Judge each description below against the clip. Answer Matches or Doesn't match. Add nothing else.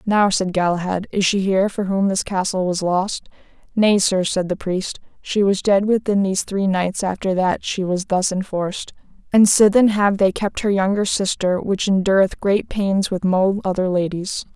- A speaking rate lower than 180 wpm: Doesn't match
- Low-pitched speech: Doesn't match